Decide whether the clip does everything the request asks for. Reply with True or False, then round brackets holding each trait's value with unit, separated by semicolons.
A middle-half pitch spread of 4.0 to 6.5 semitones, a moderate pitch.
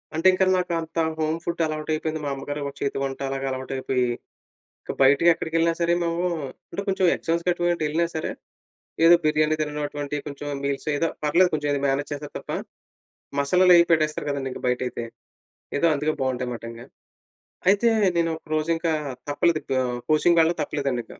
False (3.1 semitones; 155 Hz)